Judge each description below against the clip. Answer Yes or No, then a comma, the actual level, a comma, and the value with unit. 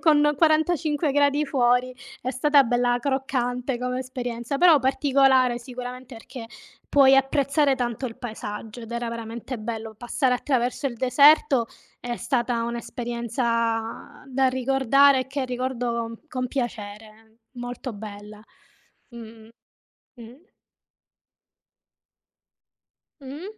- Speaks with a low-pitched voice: No, very high, 250 Hz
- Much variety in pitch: No, narrow, 2.5 semitones